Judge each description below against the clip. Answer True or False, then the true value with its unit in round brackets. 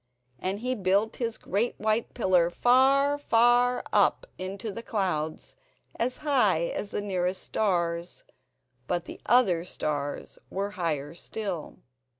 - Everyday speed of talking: False (130 wpm)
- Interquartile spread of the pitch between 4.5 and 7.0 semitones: True (5.1 semitones)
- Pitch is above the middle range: True (200 Hz)